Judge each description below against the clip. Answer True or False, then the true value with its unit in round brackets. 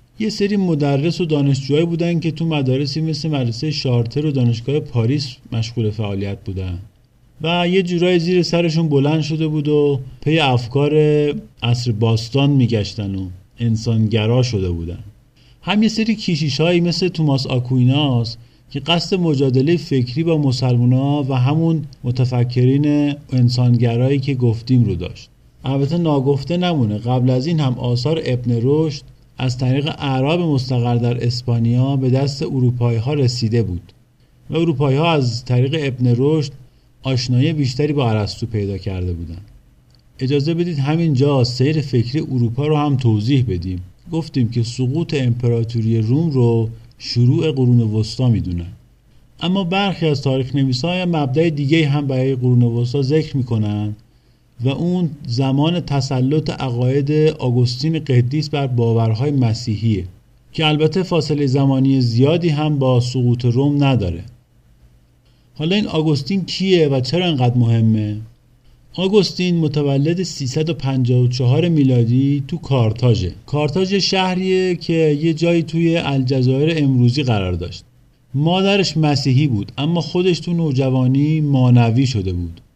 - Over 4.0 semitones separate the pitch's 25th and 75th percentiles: True (4.4 semitones)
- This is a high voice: False (135 Hz)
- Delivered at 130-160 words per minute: True (135 wpm)